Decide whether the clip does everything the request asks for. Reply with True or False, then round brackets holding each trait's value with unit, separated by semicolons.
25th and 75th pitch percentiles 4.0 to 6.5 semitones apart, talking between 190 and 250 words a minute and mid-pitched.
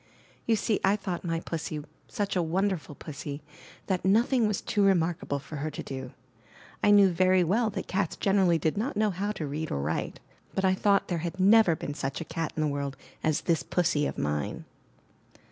True (4.4 semitones; 200 wpm; 175 Hz)